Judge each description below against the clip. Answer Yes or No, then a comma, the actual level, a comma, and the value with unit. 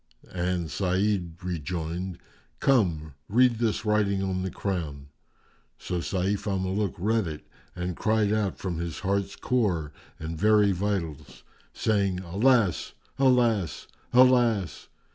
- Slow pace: Yes, slow, 120 wpm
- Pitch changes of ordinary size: Yes, average, 3.5 semitones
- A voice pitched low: Yes, very low, 95 Hz